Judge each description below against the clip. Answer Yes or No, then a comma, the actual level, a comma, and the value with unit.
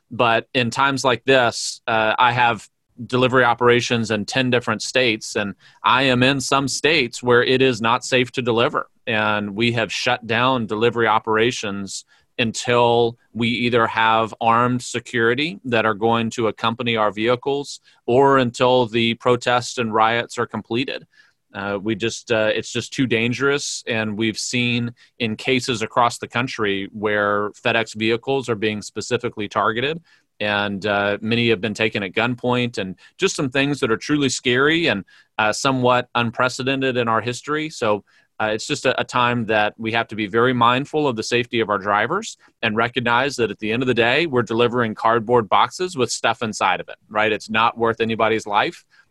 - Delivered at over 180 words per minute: No, average, 175 wpm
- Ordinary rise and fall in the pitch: No, narrow, 2.2 semitones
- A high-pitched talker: No, low, 120 Hz